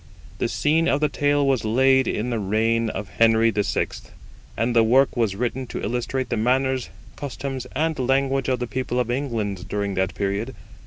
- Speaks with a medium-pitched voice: No, low, 120 Hz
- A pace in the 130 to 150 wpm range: No, average, 180 wpm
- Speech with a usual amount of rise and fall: Yes, average, 3.2 semitones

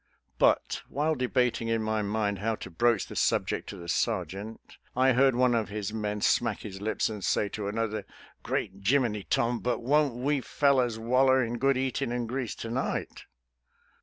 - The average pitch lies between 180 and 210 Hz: No, low, 115 Hz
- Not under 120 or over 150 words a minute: No, average, 190 wpm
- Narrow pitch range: No, average, 3.2 semitones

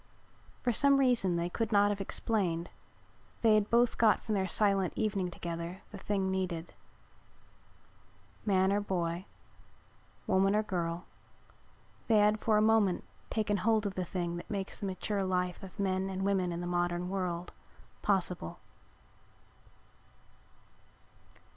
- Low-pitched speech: No, high, 195 Hz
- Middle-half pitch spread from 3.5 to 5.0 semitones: No, average, 2.9 semitones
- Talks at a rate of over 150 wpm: No, average, 140 wpm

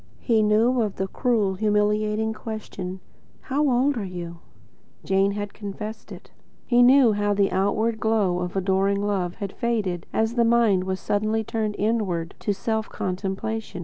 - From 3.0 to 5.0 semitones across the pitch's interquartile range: No, narrow, 2.6 semitones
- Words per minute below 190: Yes, average, 160 wpm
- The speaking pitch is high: Yes, high, 210 Hz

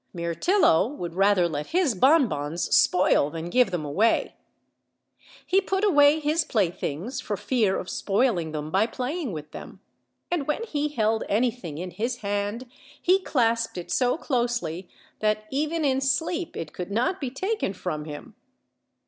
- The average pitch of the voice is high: Yes, high, 225 Hz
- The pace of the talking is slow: No, average, 165 wpm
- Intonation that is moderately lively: No, wide, 8.4 semitones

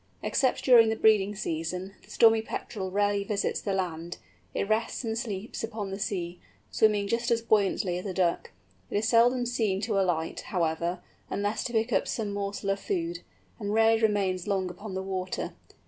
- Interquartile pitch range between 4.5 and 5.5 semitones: No, average, 3.0 semitones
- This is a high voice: Yes, high, 200 Hz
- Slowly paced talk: No, average, 180 wpm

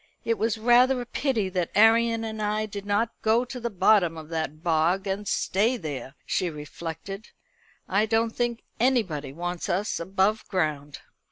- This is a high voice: Yes, high, 205 Hz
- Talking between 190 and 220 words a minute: No, average, 165 wpm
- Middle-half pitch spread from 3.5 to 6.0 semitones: Yes, average, 5.0 semitones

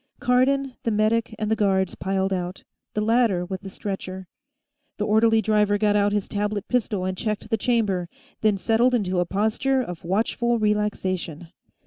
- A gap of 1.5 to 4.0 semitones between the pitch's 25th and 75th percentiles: Yes, average, 2.9 semitones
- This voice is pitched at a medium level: No, high, 210 Hz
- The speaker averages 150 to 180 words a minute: Yes, average, 165 wpm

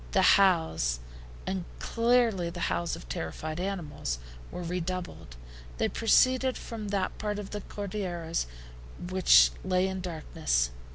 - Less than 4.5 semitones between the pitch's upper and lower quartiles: Yes, average, 3.9 semitones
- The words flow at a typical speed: No, slow, 125 wpm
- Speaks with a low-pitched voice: No, medium, 185 Hz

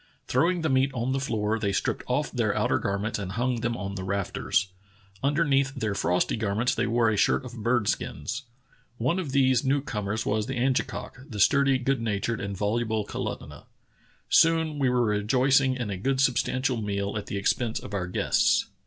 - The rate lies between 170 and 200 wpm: Yes, average, 190 wpm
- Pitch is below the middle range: Yes, low, 120 Hz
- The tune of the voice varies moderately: Yes, average, 4.4 semitones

